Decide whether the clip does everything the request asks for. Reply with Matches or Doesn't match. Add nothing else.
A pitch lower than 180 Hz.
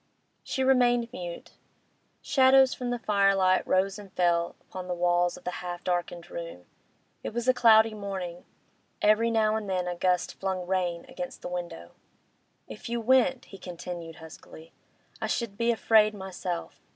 Doesn't match